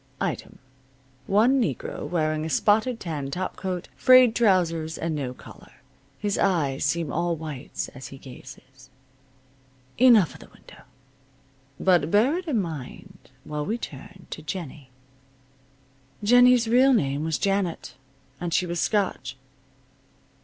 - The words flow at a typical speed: No, slow, 130 wpm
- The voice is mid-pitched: Yes, medium, 170 Hz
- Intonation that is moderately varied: No, wide, 6.1 semitones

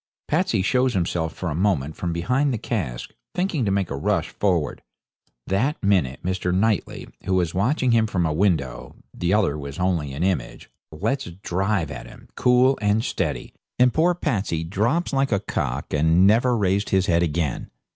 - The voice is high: No, very low, 95 Hz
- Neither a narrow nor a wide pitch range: No, wide, 5.8 semitones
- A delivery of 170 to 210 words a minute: Yes, average, 175 wpm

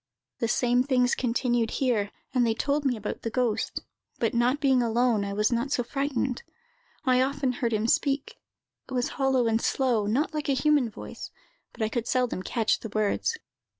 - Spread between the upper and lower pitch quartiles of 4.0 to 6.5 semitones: No, average, 2.8 semitones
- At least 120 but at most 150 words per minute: No, average, 185 wpm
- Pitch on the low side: No, high, 245 Hz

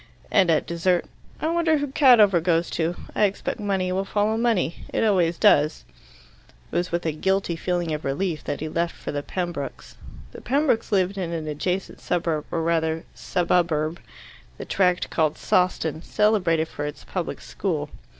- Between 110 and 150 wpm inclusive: No, average, 170 wpm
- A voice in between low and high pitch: Yes, medium, 175 Hz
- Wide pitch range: No, average, 3.4 semitones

